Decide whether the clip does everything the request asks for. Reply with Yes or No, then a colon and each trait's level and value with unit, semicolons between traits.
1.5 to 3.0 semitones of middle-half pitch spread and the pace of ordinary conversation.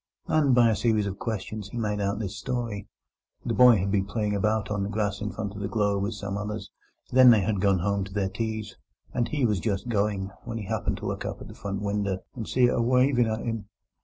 No: narrow, 2.4 semitones; fast, 250 wpm